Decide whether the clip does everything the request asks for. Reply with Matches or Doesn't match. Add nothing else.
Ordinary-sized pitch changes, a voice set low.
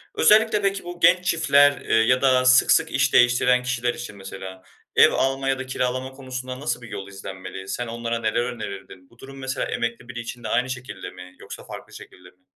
Matches